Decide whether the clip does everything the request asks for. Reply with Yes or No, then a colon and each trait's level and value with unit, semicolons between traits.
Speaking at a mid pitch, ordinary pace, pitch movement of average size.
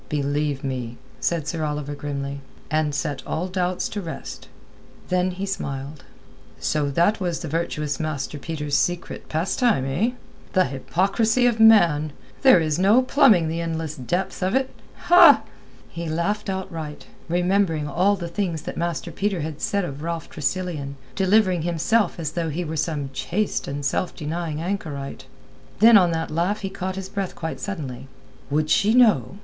Yes: medium, 165 Hz; average, 155 wpm; average, 4.4 semitones